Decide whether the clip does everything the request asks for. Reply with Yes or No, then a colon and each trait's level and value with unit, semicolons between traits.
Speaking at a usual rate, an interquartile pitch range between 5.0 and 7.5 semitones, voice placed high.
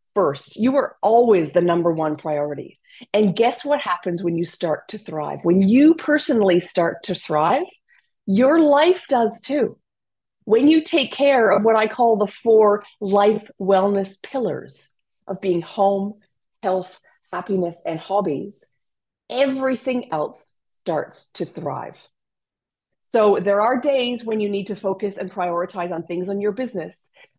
Yes: average, 150 wpm; average, 5.3 semitones; high, 205 Hz